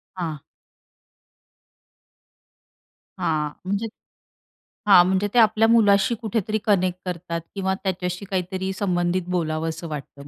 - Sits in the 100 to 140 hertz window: No, medium, 185 Hz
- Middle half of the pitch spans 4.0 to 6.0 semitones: No, average, 2.8 semitones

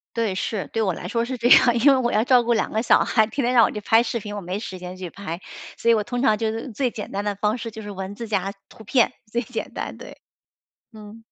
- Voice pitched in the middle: No, high, 220 Hz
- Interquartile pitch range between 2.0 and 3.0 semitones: Yes, average, 2.7 semitones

